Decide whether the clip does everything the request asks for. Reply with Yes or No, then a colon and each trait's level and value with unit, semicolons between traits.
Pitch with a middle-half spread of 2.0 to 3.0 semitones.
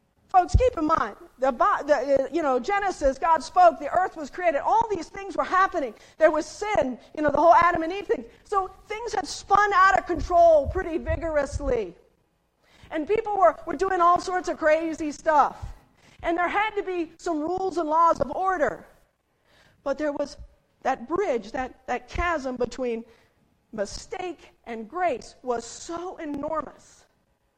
No: average, 4.2 semitones